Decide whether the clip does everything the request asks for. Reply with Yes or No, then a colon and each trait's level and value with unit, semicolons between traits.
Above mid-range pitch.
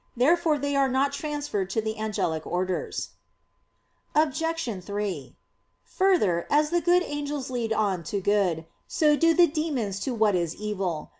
Yes: high, 240 Hz